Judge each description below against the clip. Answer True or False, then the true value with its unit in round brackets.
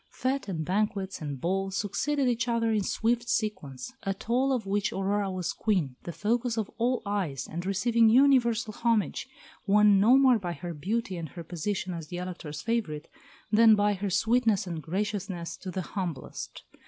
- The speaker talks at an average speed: True (175 wpm)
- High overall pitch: True (205 Hz)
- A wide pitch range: False (4.4 semitones)